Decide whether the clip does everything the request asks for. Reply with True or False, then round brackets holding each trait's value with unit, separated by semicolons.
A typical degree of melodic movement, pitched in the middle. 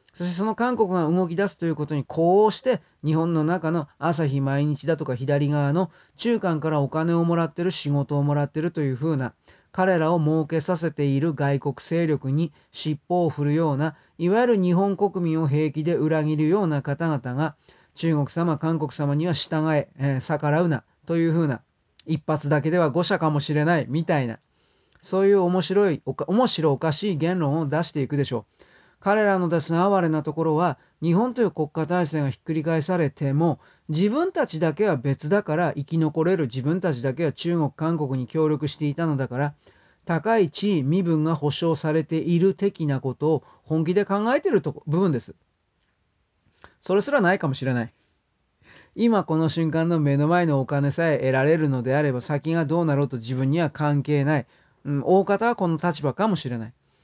True (3.3 semitones; 160 Hz)